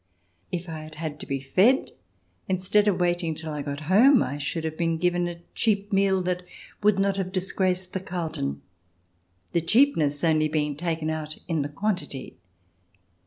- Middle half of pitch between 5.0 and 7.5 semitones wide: No, average, 3.5 semitones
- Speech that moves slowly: No, average, 175 wpm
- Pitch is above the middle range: No, medium, 170 Hz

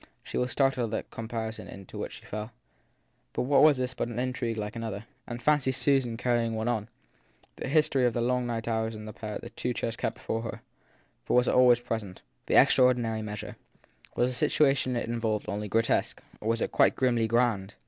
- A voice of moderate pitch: No, low, 120 Hz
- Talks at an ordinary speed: No, fast, 210 wpm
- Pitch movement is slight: Yes, narrow, 2.1 semitones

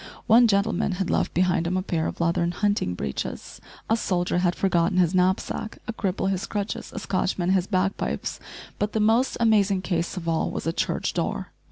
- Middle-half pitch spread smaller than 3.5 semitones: Yes, average, 2.8 semitones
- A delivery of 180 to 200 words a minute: Yes, average, 190 wpm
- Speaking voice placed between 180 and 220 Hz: Yes, medium, 185 Hz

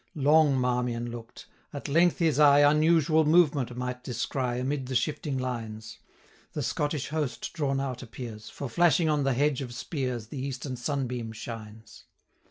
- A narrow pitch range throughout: No, average, 3.3 semitones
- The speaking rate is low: No, average, 160 wpm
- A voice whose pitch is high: No, low, 130 Hz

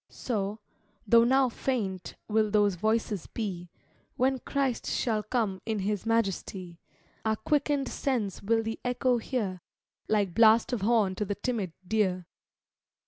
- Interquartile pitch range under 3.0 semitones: No, average, 3.4 semitones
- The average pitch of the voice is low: No, high, 220 Hz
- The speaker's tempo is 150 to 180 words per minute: No, average, 140 wpm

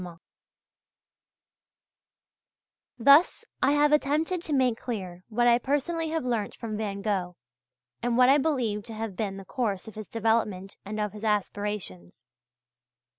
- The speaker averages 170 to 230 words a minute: No, average, 140 wpm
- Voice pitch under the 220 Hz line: No, high, 225 Hz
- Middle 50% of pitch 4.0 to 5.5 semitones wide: Yes, average, 4.9 semitones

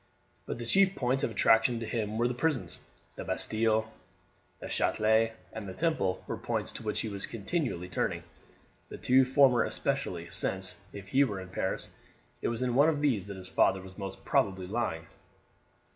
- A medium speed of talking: Yes, average, 185 wpm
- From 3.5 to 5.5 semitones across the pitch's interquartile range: Yes, average, 4.6 semitones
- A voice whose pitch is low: Yes, low, 110 Hz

